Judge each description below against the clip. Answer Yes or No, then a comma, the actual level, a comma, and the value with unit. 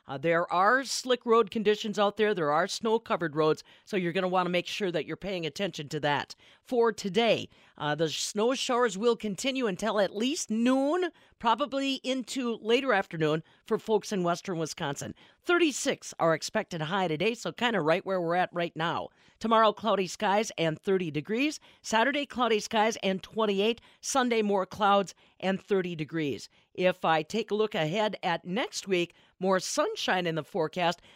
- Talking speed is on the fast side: No, average, 180 wpm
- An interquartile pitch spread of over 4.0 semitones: Yes, average, 5.0 semitones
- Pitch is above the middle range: Yes, high, 200 Hz